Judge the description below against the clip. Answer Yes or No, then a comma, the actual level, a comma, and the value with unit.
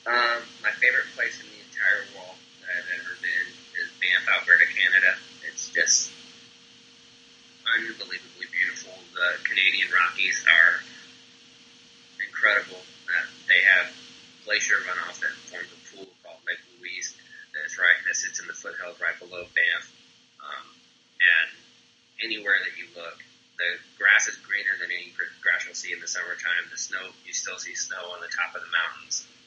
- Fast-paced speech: No, average, 155 wpm